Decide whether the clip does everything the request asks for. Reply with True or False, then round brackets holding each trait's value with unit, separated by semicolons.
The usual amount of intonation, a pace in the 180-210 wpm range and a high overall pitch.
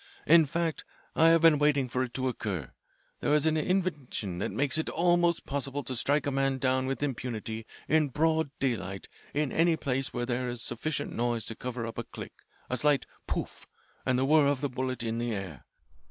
False (3.9 semitones; 200 wpm; 135 Hz)